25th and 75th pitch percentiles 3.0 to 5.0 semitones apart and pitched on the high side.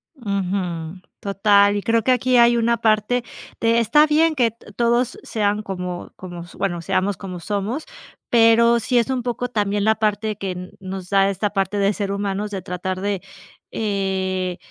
Yes: average, 3.4 semitones; high, 205 Hz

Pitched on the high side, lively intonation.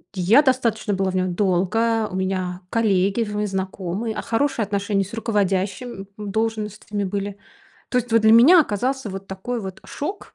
No: high, 205 Hz; average, 3.0 semitones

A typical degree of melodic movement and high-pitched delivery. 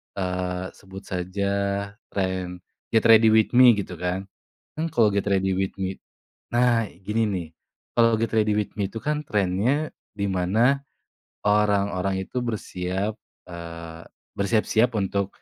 No: average, 3.2 semitones; low, 100 Hz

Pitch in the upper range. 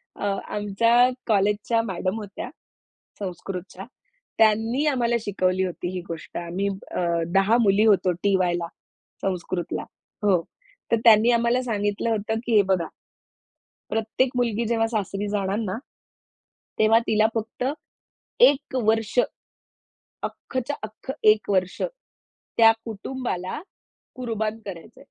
Yes: high, 215 Hz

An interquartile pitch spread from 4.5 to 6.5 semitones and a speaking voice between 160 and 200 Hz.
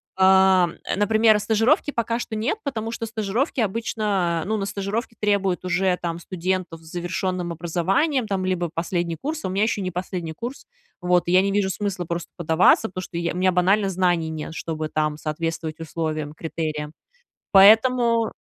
No: average, 4.1 semitones; medium, 185 Hz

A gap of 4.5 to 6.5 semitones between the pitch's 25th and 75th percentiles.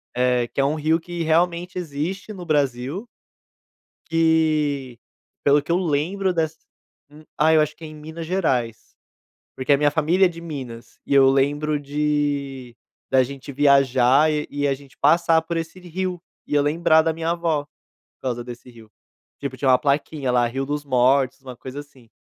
No: average, 3.3 semitones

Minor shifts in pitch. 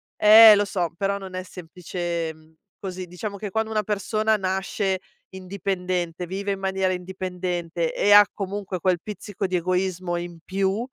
Yes: narrow, 2.0 semitones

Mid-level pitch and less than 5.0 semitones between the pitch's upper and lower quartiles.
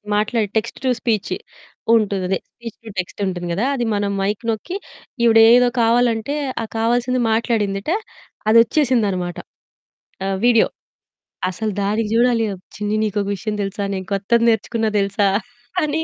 No: high, 220 Hz; average, 2.8 semitones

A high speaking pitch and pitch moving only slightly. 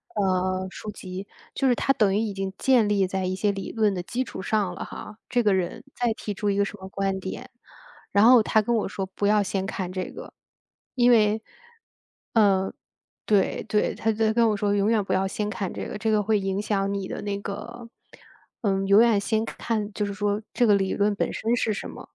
Yes: high, 205 Hz; narrow, 2.2 semitones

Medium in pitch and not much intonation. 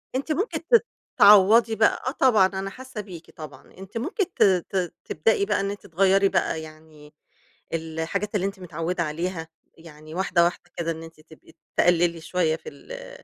No: medium, 180 Hz; average, 4.3 semitones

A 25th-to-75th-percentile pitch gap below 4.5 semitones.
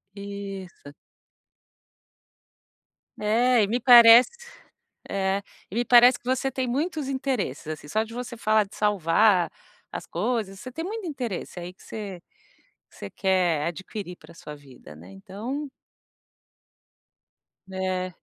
No: average, 5.1 semitones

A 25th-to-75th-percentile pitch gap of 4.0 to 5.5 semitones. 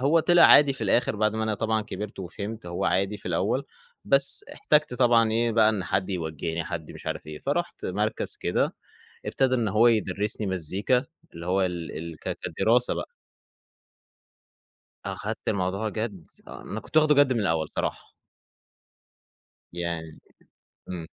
Yes: average, 4.7 semitones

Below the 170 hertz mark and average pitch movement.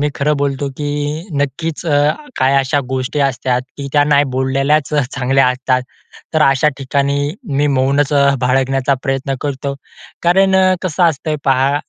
No: medium, 140 Hz; narrow, 1.7 semitones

